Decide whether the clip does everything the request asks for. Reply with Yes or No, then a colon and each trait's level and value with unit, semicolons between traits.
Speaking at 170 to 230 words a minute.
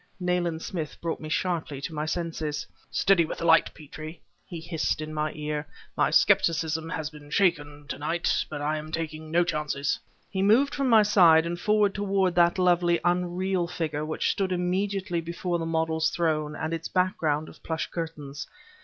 Yes: average, 180 wpm